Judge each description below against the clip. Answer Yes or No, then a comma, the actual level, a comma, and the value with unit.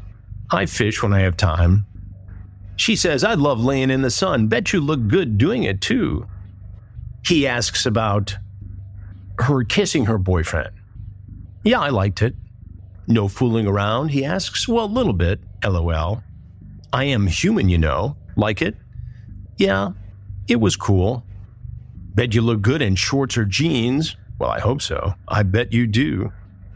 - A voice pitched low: Yes, low, 100 Hz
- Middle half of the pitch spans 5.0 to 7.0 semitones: No, average, 3.3 semitones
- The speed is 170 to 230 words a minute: No, average, 155 wpm